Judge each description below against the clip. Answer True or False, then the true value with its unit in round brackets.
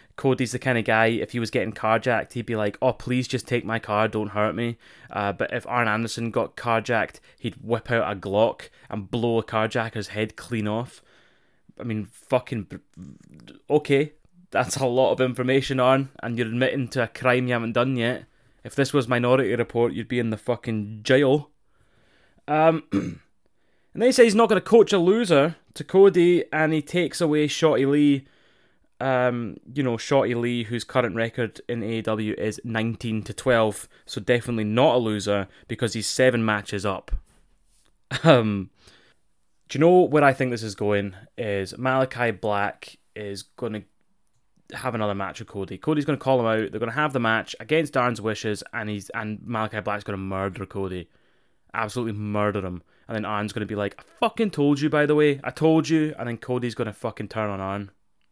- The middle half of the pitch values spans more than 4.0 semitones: False (3.7 semitones)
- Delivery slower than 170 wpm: False (190 wpm)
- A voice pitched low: True (120 Hz)